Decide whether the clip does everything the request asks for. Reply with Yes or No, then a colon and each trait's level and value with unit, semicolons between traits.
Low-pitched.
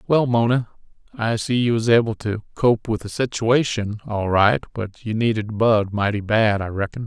Yes: low, 110 Hz